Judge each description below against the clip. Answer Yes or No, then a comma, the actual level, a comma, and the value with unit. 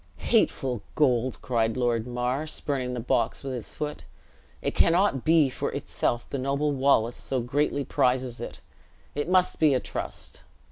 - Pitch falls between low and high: No, low, 130 Hz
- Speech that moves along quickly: No, average, 155 wpm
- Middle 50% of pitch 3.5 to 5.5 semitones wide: No, average, 3.1 semitones